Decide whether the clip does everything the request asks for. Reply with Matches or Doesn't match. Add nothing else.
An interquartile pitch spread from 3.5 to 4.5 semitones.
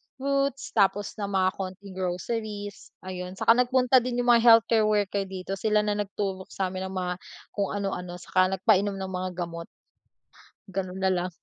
Doesn't match